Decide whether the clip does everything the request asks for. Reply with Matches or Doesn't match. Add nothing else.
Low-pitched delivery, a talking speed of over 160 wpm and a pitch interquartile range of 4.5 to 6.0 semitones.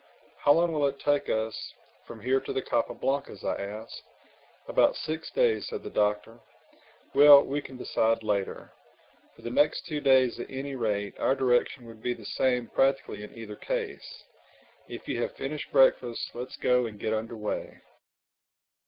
Doesn't match